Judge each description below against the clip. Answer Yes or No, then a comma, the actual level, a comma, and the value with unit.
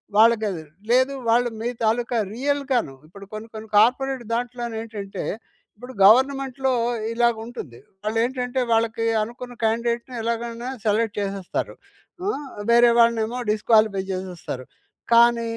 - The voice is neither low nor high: No, high, 230 Hz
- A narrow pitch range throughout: Yes, narrow, 2.1 semitones